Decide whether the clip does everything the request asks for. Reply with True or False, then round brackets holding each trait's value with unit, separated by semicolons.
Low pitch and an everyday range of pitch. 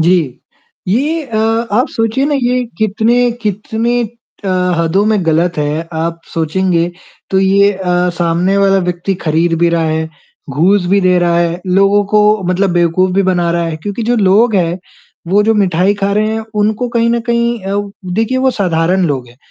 False (190 Hz; 4.2 semitones)